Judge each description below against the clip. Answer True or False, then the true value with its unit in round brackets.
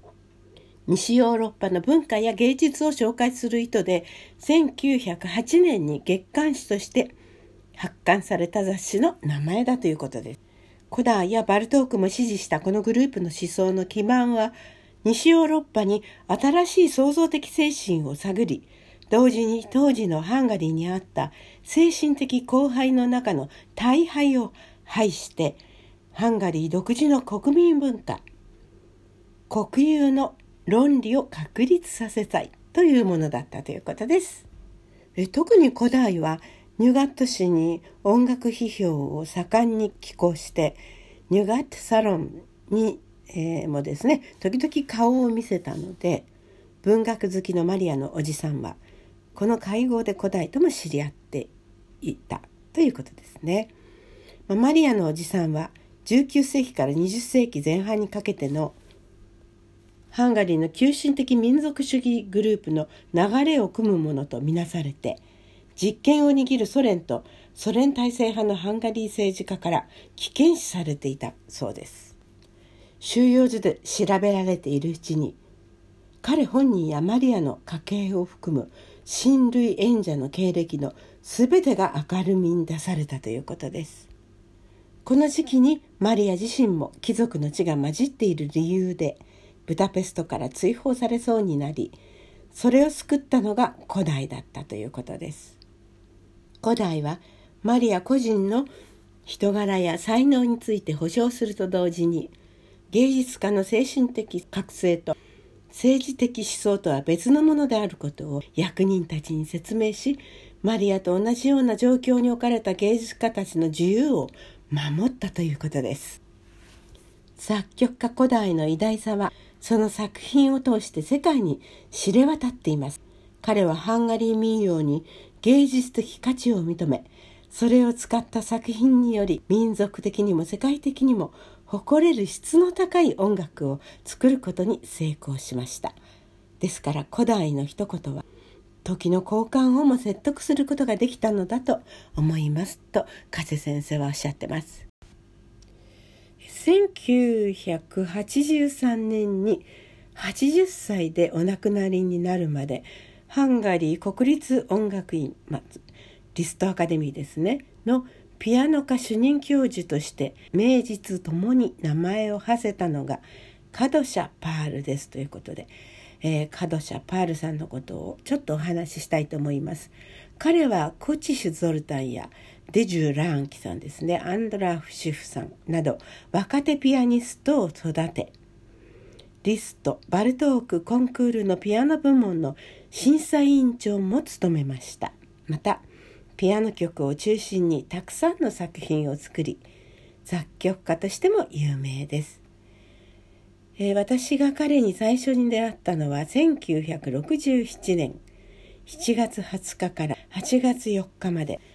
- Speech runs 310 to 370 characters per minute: False (275 characters per minute)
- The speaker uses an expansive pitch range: True (7.9 semitones)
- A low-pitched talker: False (195 Hz)